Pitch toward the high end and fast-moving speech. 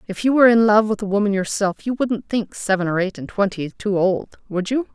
Yes: high, 205 Hz; fast, 245 wpm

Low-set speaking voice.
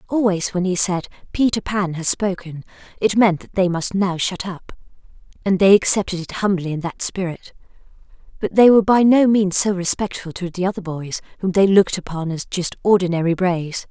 No: medium, 185 Hz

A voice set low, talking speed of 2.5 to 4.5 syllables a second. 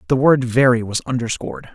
No: low, 125 Hz; 6.0 syllables/s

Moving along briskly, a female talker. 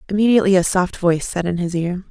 Yes: fast, 230 wpm; female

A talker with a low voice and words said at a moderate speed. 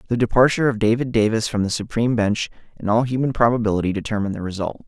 Yes: low, 115 Hz; average, 195 wpm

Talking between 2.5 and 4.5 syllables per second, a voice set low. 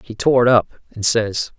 Yes: 4.4 syllables/s; low, 115 Hz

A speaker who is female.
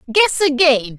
Yes: female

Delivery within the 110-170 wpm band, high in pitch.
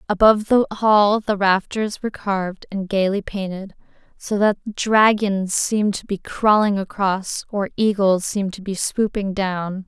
Yes: average, 150 wpm; high, 200 Hz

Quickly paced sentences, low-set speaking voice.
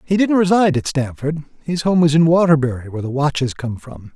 No: fast, 215 wpm; medium, 150 Hz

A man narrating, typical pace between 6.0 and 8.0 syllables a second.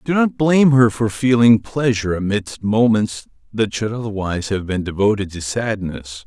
No: male; 4.9 syllables/s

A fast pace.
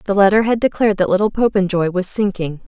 No: average, 195 wpm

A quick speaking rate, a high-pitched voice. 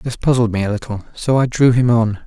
No: fast, 265 wpm; low, 115 Hz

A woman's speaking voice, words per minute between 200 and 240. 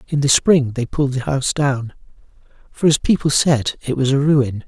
No: male; fast, 205 wpm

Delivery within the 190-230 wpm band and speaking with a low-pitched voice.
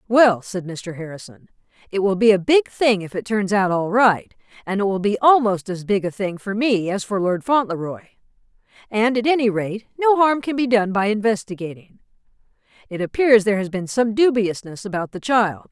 No: average, 200 wpm; high, 205 Hz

